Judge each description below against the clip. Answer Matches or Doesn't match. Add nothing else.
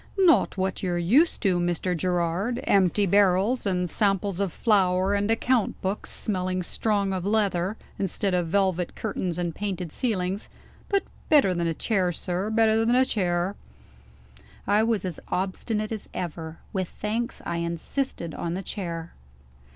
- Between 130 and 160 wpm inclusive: Matches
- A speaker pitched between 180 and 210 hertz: Matches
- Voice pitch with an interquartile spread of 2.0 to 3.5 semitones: Matches